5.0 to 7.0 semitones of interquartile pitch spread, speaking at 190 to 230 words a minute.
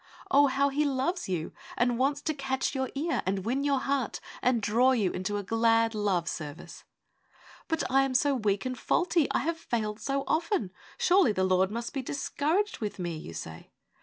Yes: wide, 5.4 semitones; average, 195 wpm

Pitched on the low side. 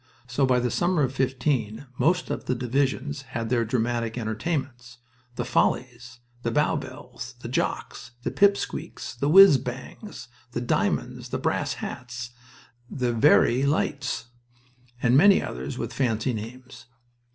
Yes: low, 125 Hz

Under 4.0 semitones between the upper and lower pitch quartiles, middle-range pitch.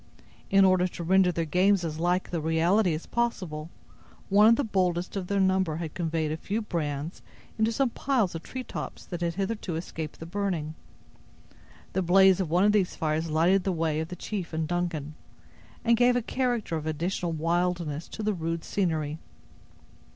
Yes: average, 3.5 semitones; medium, 175 Hz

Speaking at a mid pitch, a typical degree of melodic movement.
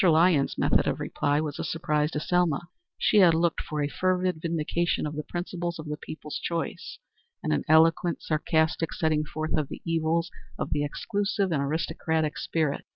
No: medium, 160 Hz; narrow, 2.2 semitones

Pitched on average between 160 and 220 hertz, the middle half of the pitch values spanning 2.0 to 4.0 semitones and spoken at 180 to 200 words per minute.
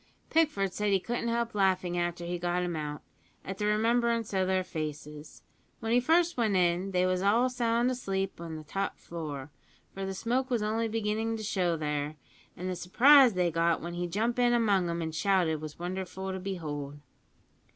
No: high, 190 Hz; average, 4.8 semitones; average, 195 wpm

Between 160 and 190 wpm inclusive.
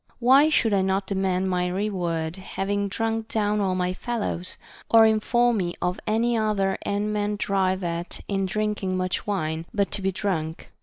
Yes: average, 175 wpm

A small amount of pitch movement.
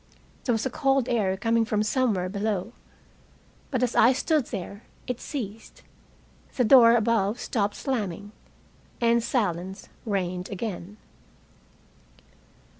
No: average, 3.5 semitones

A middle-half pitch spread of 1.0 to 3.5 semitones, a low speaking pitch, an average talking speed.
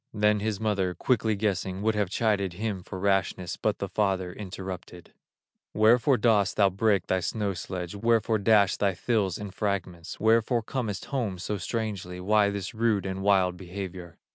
Yes: narrow, 2.5 semitones; low, 100 Hz; average, 165 wpm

